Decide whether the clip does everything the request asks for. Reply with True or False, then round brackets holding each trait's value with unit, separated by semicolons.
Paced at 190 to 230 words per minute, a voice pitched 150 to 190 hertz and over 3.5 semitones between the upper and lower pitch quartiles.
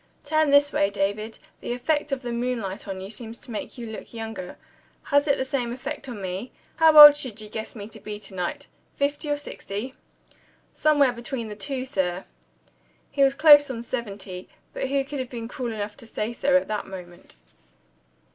False (195 wpm; 240 Hz; 5.0 semitones)